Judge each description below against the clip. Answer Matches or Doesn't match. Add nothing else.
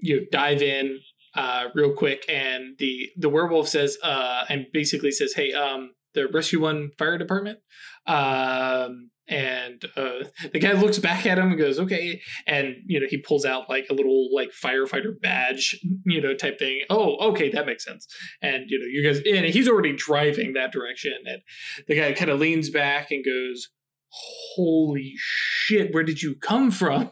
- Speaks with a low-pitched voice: Doesn't match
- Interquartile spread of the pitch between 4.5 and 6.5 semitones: Matches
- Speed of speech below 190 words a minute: Matches